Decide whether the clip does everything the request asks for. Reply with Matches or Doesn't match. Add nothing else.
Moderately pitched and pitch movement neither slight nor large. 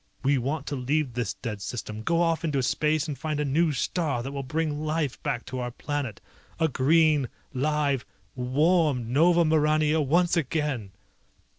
Matches